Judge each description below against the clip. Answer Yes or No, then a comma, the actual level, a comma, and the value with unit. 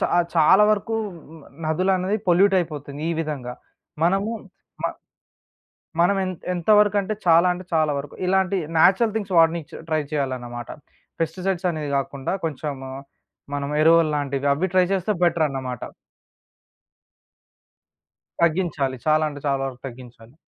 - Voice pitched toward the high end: No, medium, 160 Hz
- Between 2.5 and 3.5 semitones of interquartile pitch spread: No, average, 4.8 semitones